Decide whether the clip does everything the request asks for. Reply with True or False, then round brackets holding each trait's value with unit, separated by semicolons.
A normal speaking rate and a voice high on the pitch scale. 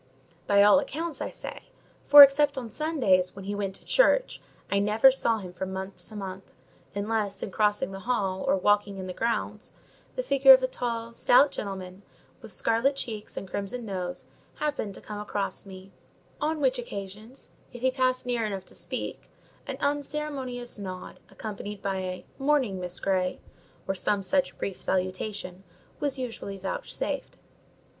True (165 wpm; 210 Hz)